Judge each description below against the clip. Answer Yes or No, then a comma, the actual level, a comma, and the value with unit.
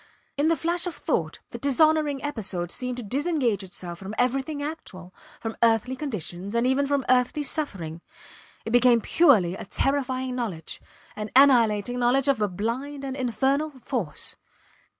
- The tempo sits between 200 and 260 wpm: No, average, 150 wpm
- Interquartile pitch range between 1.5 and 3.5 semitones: No, average, 5.0 semitones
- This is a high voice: Yes, very high, 250 Hz